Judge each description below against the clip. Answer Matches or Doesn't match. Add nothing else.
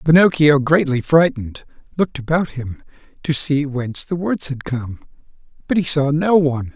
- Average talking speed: Matches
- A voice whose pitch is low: Doesn't match